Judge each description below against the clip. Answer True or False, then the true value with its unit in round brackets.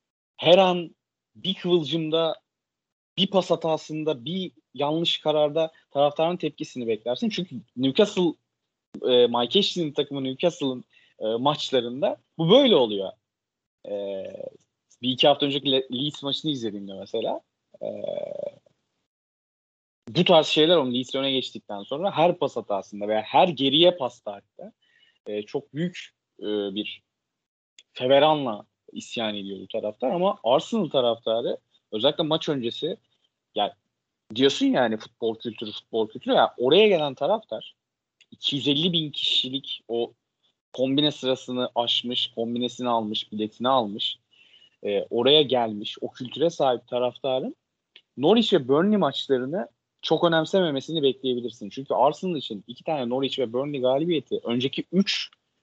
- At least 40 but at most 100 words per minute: False (125 wpm)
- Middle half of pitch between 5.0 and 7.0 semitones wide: True (5.4 semitones)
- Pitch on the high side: False (140 Hz)